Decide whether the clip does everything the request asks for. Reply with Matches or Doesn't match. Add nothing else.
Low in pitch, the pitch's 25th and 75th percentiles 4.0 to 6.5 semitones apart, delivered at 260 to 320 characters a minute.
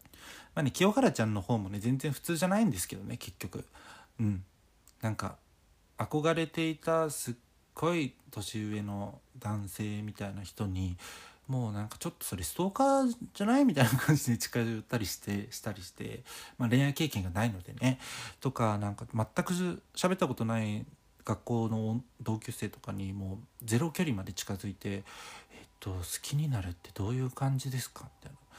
Doesn't match